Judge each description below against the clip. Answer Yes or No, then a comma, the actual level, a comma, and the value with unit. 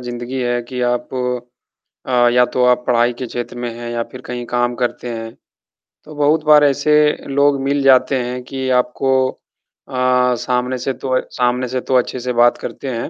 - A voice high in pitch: No, low, 125 Hz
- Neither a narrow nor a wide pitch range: No, narrow, 1.5 semitones